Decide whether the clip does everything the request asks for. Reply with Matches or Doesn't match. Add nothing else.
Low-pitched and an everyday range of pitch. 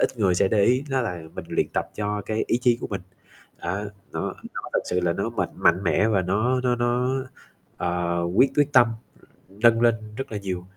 Matches